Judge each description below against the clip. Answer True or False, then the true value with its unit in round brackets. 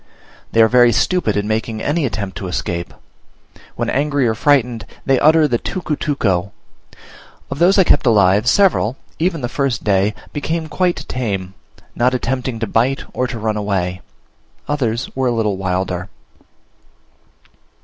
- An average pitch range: False (5.7 semitones)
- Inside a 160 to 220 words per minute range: False (150 wpm)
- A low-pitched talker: True (120 Hz)